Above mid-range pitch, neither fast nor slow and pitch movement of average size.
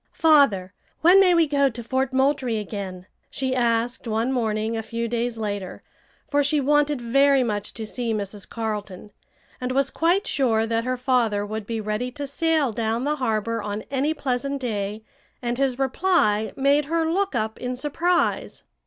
Yes: high, 245 Hz; average, 170 wpm; average, 4.3 semitones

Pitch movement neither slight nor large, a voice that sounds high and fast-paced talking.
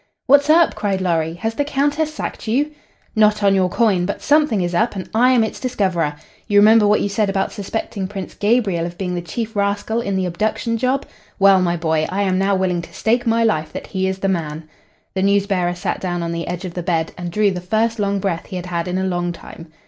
Yes: average, 3.9 semitones; high, 195 Hz; fast, 240 wpm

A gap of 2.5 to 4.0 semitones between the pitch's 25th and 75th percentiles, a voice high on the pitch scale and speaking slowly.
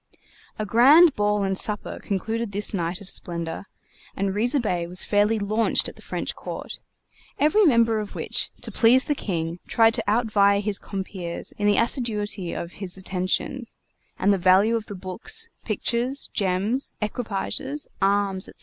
No: average, 3.4 semitones; high, 205 Hz; average, 160 wpm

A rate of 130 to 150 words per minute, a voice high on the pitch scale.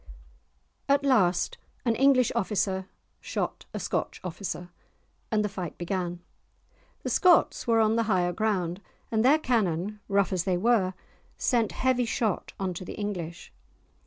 Yes: average, 145 wpm; high, 205 Hz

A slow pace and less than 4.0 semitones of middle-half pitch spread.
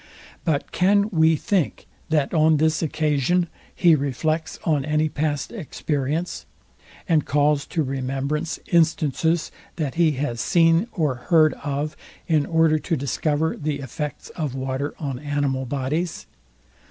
Yes: slow, 130 wpm; narrow, 2.5 semitones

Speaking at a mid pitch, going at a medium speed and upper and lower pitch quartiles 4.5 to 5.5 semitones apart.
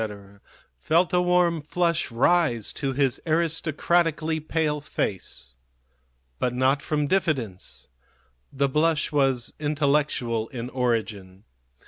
No: medium, 145 Hz; slow, 100 wpm; average, 4.8 semitones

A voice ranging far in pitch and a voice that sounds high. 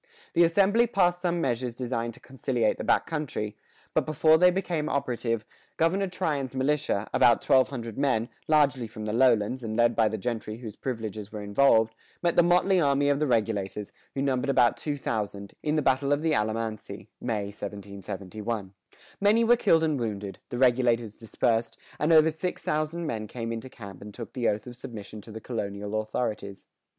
No: wide, 5.7 semitones; low, 120 Hz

